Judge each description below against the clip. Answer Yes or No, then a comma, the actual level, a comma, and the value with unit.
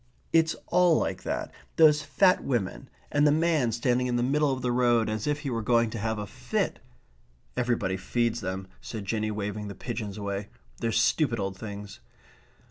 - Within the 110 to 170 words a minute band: No, average, 190 wpm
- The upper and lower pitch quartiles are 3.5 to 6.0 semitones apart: Yes, average, 4.5 semitones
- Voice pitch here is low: Yes, low, 115 Hz